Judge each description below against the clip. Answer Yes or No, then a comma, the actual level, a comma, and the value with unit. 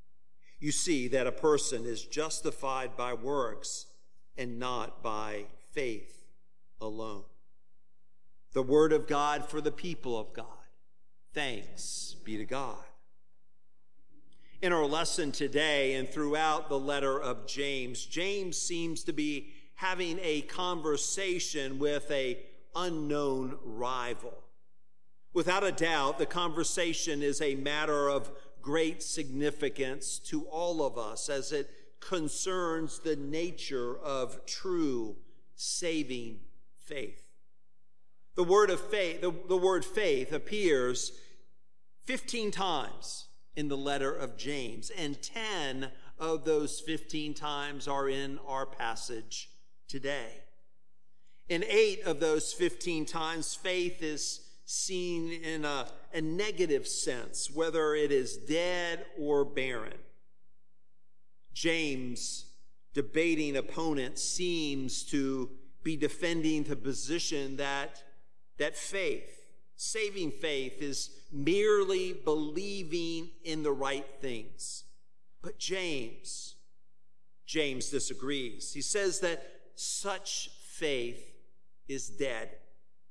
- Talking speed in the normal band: No, slow, 110 wpm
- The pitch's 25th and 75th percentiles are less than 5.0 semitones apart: Yes, average, 4.1 semitones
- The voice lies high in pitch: No, medium, 145 Hz